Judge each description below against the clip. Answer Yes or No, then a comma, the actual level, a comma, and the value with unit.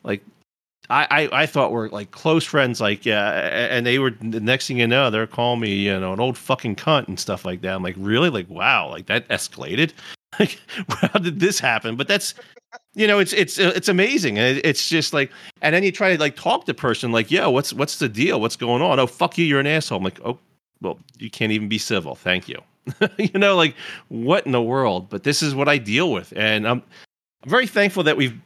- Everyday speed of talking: No, fast, 240 wpm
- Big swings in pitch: Yes, wide, 7.3 semitones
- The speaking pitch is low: Yes, low, 130 Hz